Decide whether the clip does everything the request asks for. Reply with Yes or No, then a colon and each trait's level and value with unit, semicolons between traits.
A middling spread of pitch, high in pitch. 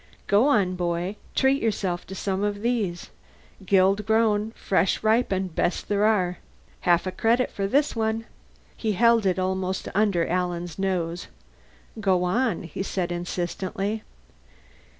Yes: average, 3.4 semitones; high, 195 Hz